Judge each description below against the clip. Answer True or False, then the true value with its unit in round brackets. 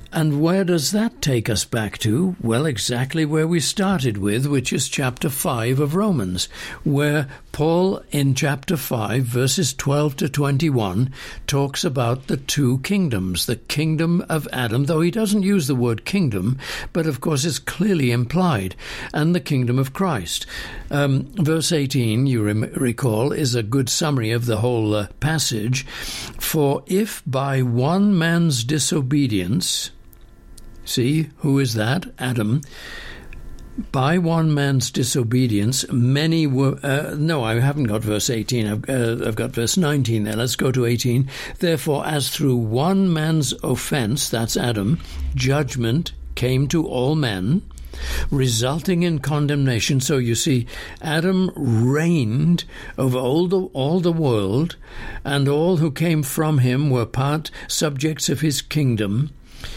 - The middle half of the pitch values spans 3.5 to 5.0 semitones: True (4.7 semitones)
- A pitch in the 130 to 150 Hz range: True (140 Hz)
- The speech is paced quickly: False (145 wpm)